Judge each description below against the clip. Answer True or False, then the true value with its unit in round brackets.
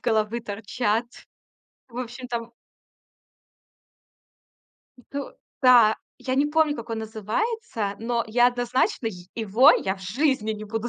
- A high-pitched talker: True (235 Hz)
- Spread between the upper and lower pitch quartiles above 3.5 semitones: False (2.8 semitones)